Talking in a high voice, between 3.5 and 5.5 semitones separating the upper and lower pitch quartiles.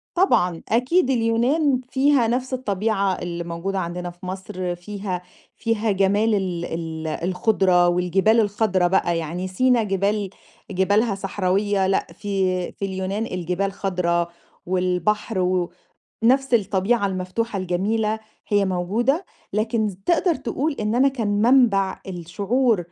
Yes: high, 195 Hz; average, 3.8 semitones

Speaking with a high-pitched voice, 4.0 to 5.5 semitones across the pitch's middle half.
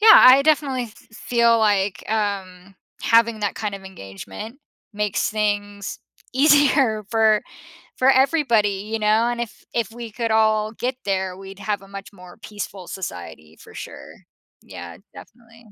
No: high, 215 Hz; average, 3.2 semitones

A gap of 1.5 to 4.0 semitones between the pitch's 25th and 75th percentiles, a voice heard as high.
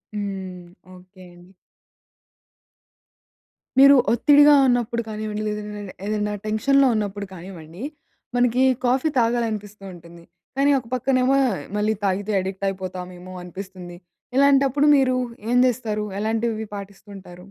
No: average, 4.5 semitones; high, 210 Hz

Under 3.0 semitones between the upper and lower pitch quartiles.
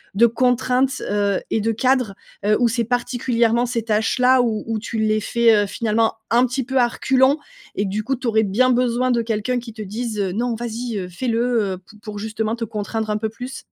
Yes: narrow, 2.4 semitones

